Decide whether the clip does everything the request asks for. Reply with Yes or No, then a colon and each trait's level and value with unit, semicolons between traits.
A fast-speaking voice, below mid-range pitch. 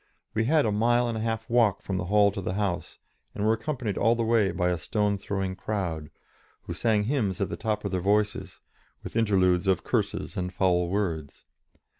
Yes: fast, 210 wpm; low, 100 Hz